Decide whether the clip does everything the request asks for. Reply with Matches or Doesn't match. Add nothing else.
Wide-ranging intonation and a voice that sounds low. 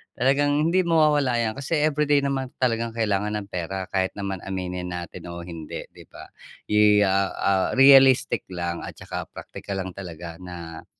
Matches